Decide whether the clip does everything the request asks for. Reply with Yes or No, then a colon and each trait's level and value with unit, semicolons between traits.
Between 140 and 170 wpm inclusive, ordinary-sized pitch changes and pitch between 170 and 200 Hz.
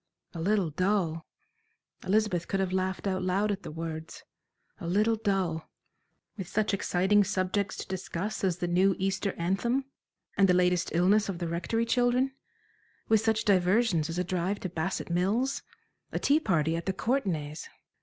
Yes: average, 165 wpm; average, 3.1 semitones; high, 190 Hz